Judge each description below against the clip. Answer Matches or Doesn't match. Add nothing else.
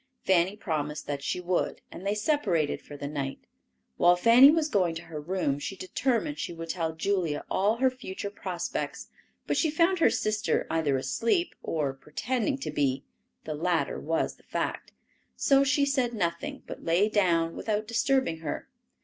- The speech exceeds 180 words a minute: Doesn't match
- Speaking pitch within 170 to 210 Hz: Matches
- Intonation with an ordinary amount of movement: Doesn't match